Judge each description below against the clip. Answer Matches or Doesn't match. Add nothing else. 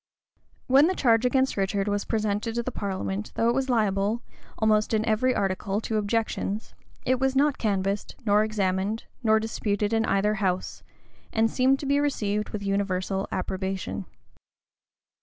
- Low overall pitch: Doesn't match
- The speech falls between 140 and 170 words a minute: Matches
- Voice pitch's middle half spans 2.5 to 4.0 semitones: Matches